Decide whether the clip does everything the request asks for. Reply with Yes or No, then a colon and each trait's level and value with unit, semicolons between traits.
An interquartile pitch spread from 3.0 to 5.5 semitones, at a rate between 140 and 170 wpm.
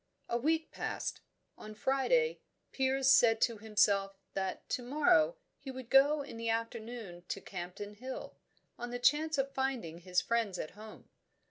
Yes: average, 4.7 semitones; average, 155 wpm